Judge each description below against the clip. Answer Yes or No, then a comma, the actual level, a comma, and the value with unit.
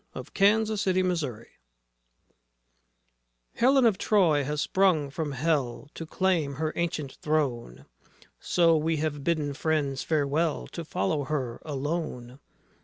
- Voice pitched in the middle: Yes, medium, 155 Hz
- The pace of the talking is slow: Yes, slow, 125 wpm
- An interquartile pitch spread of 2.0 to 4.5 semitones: Yes, average, 3.4 semitones